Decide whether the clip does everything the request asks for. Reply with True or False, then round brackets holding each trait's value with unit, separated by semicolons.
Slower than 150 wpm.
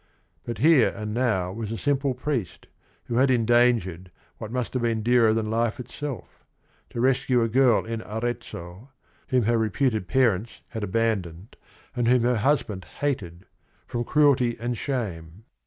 False (155 wpm)